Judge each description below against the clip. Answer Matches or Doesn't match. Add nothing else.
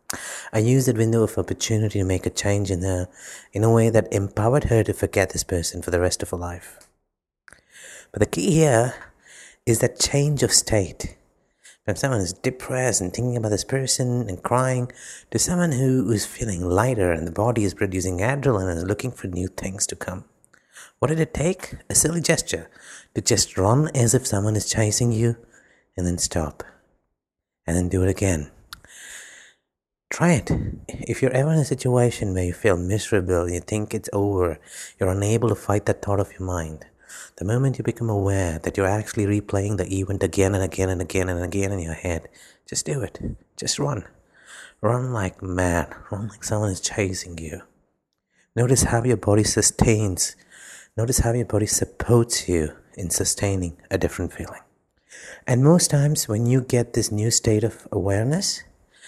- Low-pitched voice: Matches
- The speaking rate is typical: Matches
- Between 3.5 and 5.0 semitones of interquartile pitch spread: Matches